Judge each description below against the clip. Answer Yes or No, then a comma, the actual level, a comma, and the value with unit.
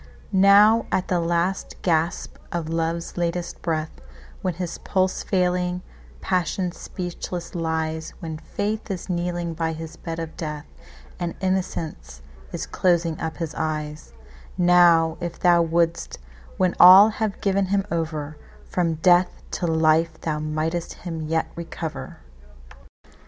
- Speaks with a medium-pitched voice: Yes, medium, 170 Hz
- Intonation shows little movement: Yes, narrow, 2.0 semitones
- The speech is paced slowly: Yes, slow, 120 wpm